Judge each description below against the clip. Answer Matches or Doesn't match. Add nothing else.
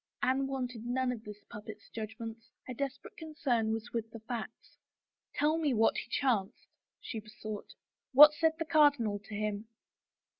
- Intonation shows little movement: Doesn't match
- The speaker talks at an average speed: Matches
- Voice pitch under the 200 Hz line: Doesn't match